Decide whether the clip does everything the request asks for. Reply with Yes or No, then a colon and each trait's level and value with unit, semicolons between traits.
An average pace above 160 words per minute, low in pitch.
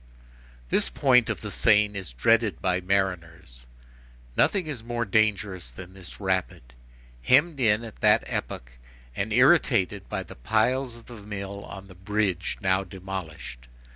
No: average, 145 wpm; low, 100 Hz